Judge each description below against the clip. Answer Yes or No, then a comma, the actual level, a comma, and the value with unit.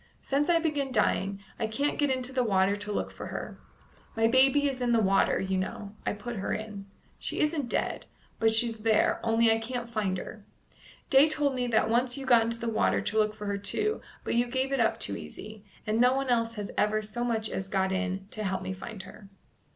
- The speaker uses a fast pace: Yes, fast, 230 wpm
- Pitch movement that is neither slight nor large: Yes, average, 3.7 semitones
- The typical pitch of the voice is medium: No, high, 225 Hz